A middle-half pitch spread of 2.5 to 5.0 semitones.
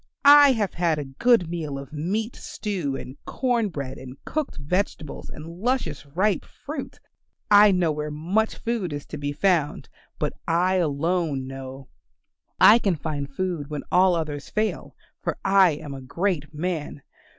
No: wide, 5.5 semitones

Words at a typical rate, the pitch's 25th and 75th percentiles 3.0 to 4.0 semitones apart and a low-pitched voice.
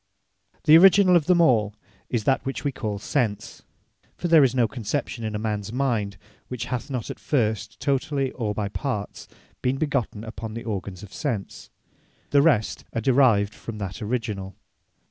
No: average, 170 wpm; average, 4.7 semitones; low, 115 Hz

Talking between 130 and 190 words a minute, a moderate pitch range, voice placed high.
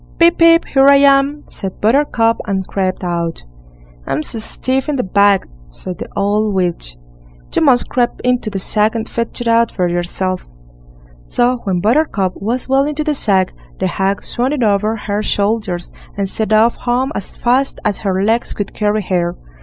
Yes: average, 180 wpm; average, 4.6 semitones; high, 215 Hz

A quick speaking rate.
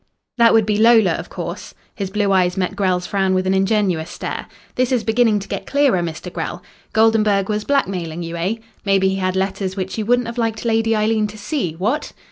Yes: fast, 210 wpm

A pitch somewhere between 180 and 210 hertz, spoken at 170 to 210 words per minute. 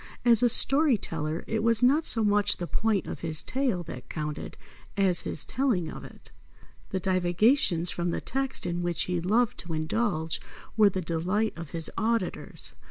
Yes: medium, 185 Hz; average, 175 wpm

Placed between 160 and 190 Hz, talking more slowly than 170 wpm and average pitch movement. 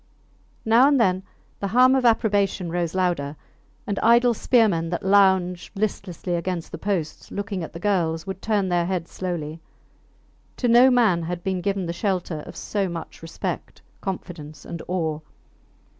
Yes: medium, 185 Hz; average, 160 wpm; average, 3.3 semitones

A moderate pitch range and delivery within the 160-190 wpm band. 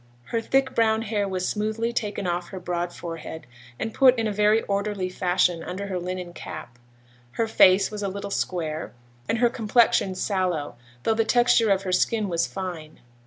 Yes: average, 3.6 semitones; average, 180 wpm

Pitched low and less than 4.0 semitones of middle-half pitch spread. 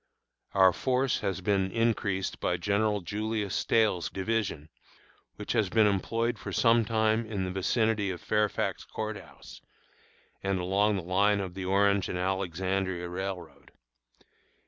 Yes: low, 100 Hz; narrow, 2.6 semitones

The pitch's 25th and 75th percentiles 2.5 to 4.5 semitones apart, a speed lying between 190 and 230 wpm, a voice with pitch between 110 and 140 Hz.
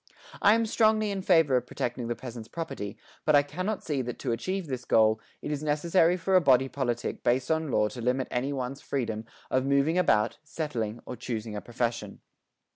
No: wide, 5.5 semitones; average, 200 wpm; low, 135 Hz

